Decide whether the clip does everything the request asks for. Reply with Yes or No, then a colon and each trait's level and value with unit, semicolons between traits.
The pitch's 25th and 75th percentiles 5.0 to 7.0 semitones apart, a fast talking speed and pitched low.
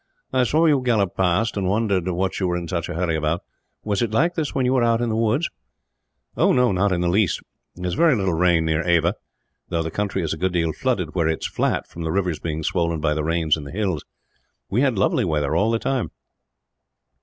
Yes: wide, 5.4 semitones; fast, 235 wpm; very low, 90 Hz